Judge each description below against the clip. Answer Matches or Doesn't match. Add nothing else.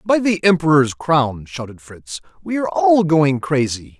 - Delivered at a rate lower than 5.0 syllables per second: Matches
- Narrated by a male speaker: Matches